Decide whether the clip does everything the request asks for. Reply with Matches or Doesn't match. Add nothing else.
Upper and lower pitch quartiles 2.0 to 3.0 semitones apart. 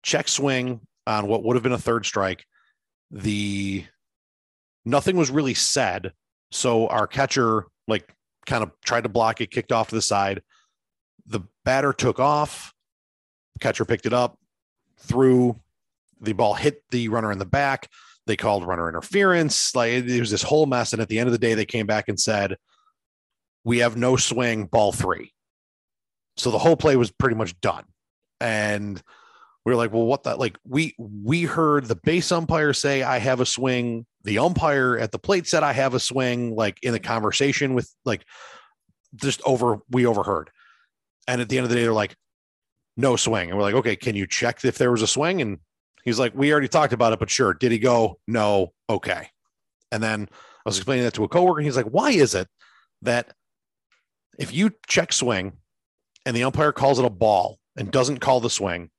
Doesn't match